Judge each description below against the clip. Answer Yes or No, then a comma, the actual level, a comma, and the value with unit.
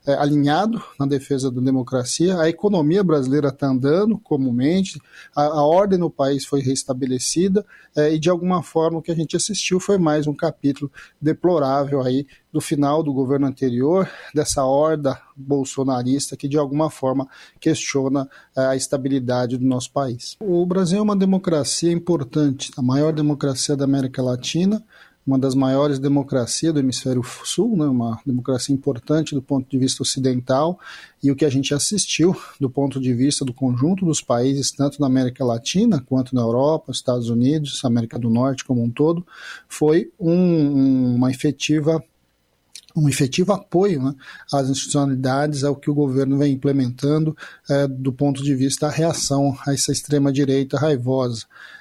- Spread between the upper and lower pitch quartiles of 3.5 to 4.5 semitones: No, average, 2.8 semitones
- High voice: No, medium, 140 Hz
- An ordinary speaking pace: Yes, average, 160 wpm